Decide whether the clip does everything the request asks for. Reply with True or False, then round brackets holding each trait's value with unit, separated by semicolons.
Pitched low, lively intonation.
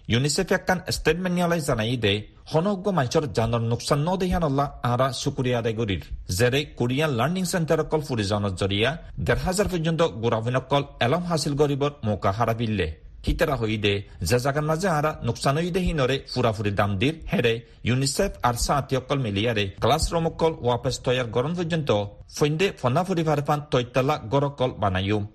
True (130 Hz; 5.7 semitones)